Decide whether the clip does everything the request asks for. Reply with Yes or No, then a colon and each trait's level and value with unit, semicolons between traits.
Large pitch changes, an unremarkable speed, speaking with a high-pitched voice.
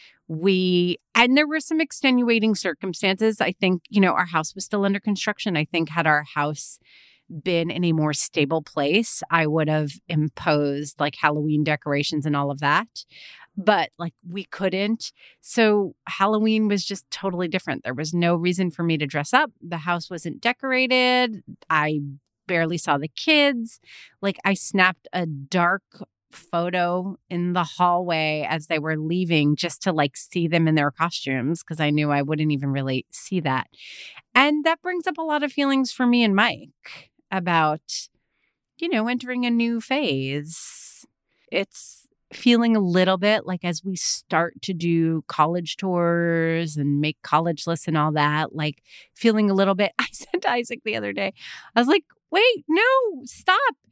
No: wide, 5.8 semitones; average, 170 wpm; medium, 175 Hz